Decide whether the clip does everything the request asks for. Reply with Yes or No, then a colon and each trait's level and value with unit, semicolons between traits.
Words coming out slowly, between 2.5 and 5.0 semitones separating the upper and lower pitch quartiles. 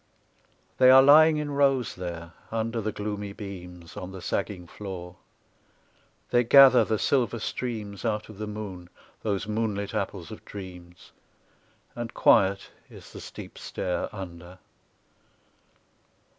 Yes: slow, 130 wpm; average, 4.1 semitones